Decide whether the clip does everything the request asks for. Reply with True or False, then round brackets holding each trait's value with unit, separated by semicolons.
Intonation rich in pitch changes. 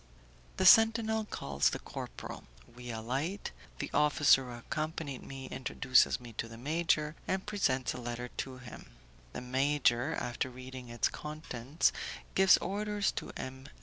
False (4.7 semitones)